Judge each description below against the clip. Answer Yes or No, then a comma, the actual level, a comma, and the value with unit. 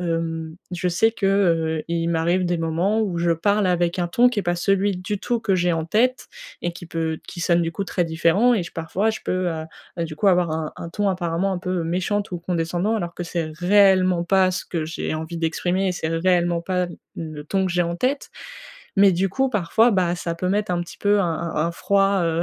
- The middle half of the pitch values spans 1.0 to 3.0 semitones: Yes, average, 2.7 semitones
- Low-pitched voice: No, medium, 175 Hz